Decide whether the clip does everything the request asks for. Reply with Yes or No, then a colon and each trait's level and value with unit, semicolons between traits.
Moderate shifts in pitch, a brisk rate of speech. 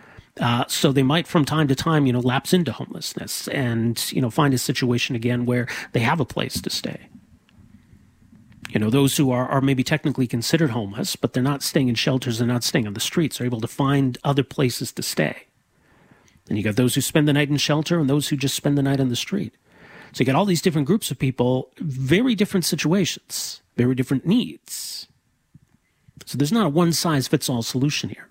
Yes: average, 3.9 semitones; fast, 215 wpm